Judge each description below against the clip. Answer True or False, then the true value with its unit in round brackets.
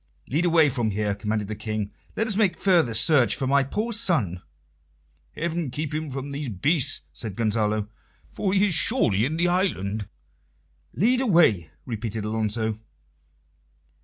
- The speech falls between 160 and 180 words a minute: False (150 wpm)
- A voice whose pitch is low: True (130 Hz)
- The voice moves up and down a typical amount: False (8.0 semitones)